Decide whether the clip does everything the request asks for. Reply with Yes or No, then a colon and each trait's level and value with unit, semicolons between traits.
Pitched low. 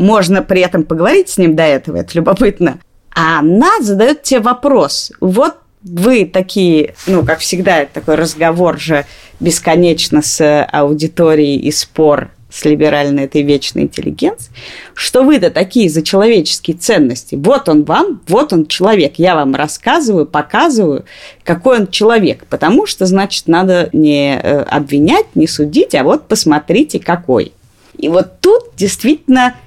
No: medium, 170 Hz